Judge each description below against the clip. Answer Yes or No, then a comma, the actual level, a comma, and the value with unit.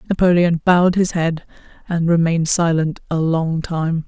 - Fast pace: No, average, 145 wpm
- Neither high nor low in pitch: Yes, medium, 170 Hz